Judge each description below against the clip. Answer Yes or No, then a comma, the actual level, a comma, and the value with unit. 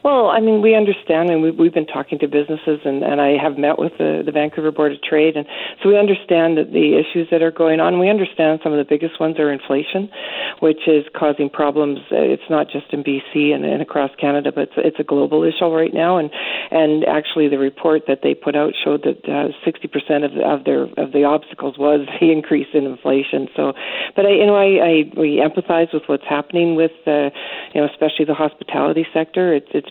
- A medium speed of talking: No, fast, 225 wpm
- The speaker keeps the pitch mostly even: Yes, narrow, 2.2 semitones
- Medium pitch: Yes, medium, 155 Hz